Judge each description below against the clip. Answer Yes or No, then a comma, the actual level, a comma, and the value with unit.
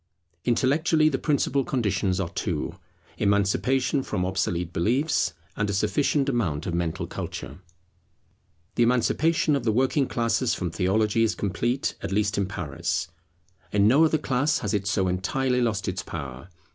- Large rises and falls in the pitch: Yes, wide, 6.0 semitones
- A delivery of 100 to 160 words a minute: Yes, average, 150 wpm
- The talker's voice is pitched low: Yes, low, 110 Hz